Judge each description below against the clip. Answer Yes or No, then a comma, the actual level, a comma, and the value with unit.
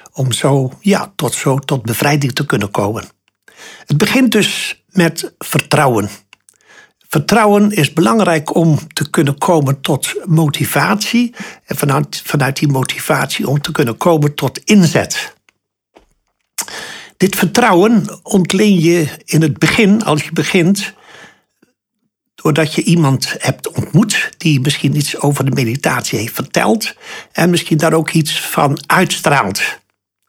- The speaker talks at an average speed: No, slow, 130 wpm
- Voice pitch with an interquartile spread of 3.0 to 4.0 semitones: No, average, 5.1 semitones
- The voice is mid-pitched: Yes, medium, 160 Hz